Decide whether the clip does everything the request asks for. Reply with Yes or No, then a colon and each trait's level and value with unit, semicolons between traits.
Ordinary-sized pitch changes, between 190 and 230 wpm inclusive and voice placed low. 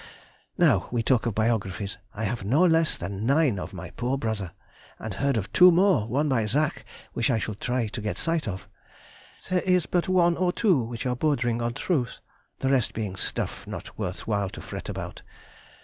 No: wide, 6.5 semitones; average, 195 wpm; low, 120 Hz